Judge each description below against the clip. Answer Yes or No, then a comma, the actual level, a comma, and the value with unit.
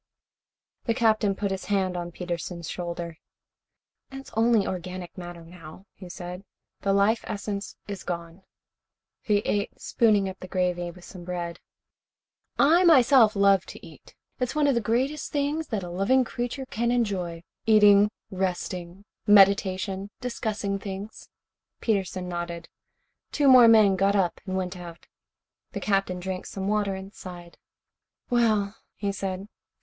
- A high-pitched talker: Yes, high, 195 Hz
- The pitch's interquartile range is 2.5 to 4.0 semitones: Yes, average, 3.4 semitones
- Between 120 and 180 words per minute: Yes, average, 145 wpm